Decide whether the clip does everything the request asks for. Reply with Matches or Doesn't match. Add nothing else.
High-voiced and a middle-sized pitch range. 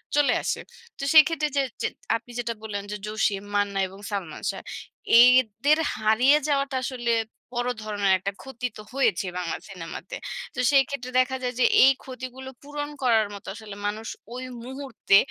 Matches